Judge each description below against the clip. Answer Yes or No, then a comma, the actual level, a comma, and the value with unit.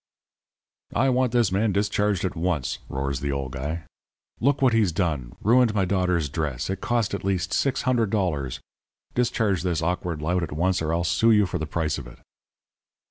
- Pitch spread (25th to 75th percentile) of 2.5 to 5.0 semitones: No, wide, 5.4 semitones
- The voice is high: No, very low, 90 Hz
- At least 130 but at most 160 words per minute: No, average, 180 wpm